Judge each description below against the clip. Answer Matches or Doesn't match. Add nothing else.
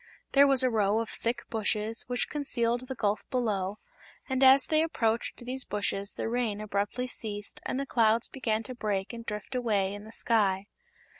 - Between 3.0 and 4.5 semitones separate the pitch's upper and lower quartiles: Matches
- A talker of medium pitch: Doesn't match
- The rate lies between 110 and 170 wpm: Doesn't match